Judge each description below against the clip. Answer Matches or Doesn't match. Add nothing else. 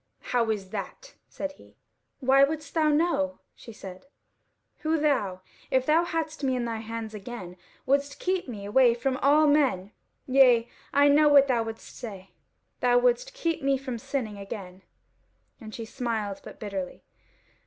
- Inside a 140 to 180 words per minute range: Matches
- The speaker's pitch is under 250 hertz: Doesn't match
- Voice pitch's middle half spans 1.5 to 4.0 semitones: Doesn't match